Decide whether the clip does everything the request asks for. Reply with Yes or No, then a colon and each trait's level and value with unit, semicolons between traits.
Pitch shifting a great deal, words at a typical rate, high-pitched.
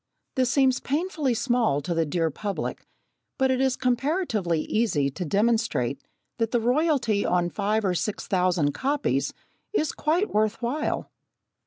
Yes: wide, 6.8 semitones; average, 145 wpm; high, 225 Hz